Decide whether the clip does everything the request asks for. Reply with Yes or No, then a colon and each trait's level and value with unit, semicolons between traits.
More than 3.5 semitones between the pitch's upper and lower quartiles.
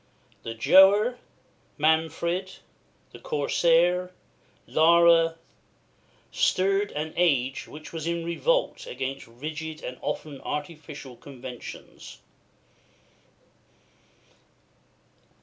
No: average, 3.2 semitones